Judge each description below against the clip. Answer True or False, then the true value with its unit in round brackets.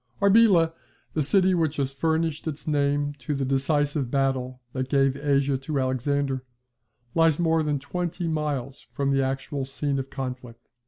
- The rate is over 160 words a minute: False (155 wpm)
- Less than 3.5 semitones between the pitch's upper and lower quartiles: True (2.8 semitones)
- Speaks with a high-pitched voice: False (140 Hz)